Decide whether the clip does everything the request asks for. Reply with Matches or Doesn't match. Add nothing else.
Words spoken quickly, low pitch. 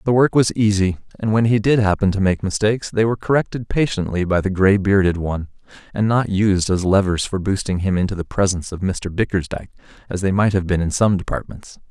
Matches